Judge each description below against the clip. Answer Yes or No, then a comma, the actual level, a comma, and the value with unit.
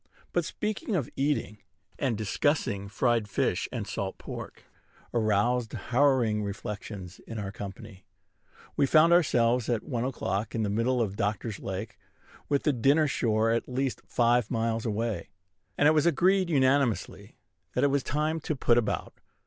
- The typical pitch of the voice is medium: No, low, 120 Hz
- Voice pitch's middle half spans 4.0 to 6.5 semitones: Yes, average, 4.8 semitones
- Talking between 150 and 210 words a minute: Yes, average, 155 wpm